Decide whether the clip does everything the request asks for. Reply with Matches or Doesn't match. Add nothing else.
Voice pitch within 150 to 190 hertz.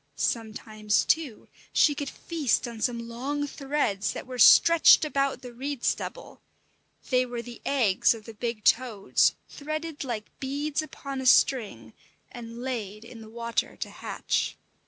Doesn't match